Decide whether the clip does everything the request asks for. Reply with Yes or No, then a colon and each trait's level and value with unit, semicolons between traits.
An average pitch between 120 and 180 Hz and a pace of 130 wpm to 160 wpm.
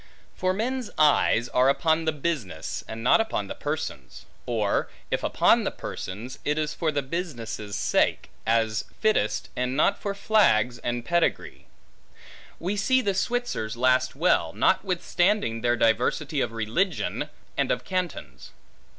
Yes: medium, 140 Hz; average, 140 wpm